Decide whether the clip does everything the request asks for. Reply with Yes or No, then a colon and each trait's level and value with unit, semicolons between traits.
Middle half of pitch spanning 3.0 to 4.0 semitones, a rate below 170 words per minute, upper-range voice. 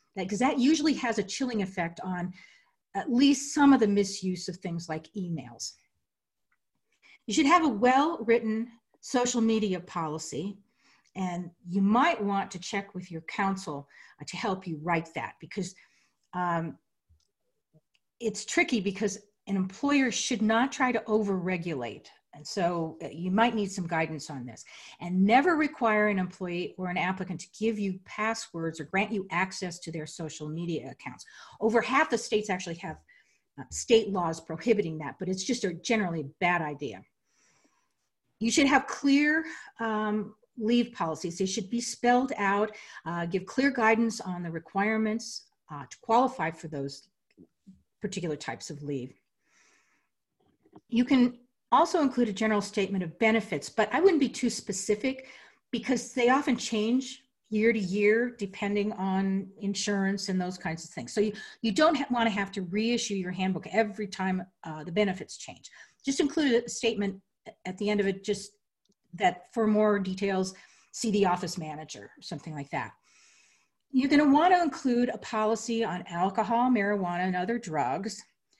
No: average, 4.6 semitones; average, 160 wpm; high, 205 Hz